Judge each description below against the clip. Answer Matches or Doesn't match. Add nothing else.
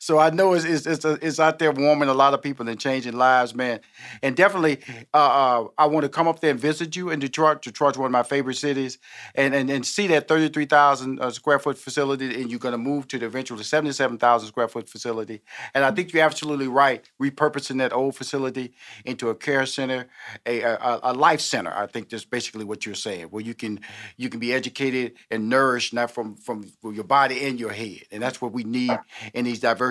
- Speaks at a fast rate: Matches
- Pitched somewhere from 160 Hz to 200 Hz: Doesn't match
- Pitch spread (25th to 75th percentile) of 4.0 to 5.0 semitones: Doesn't match